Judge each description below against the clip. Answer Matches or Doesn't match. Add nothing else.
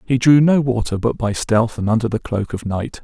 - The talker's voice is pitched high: Doesn't match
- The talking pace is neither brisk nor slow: Doesn't match